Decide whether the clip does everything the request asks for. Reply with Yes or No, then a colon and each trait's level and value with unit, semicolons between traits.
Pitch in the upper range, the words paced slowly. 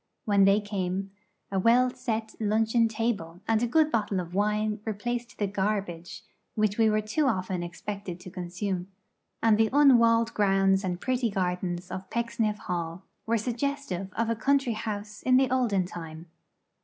No: high, 210 Hz; average, 160 wpm